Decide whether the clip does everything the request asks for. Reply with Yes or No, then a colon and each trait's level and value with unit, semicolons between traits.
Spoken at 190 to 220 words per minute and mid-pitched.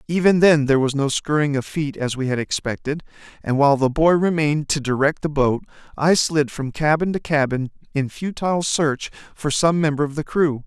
Yes: average, 200 wpm; medium, 150 Hz